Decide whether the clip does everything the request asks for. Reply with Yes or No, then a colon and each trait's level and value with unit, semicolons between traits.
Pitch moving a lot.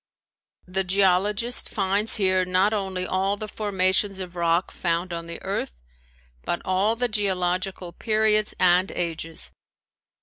No: narrow, 2.4 semitones